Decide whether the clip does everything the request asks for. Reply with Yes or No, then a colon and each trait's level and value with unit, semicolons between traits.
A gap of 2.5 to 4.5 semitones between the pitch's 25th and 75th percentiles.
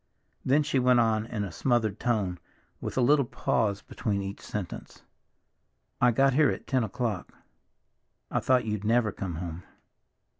Yes: average, 3.9 semitones